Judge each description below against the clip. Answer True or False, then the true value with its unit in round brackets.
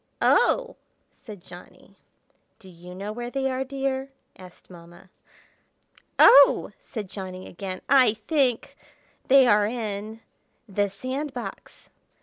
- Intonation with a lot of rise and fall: True (5.8 semitones)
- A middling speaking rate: False (110 wpm)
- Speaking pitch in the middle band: False (220 Hz)